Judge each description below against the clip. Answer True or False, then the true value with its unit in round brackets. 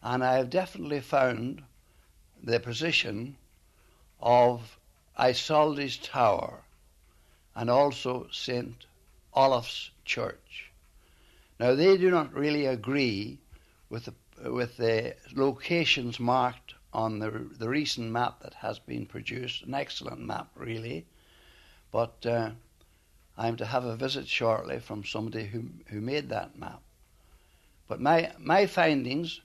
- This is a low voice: True (120 Hz)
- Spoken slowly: True (120 wpm)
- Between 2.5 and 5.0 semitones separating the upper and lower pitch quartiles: False (5.5 semitones)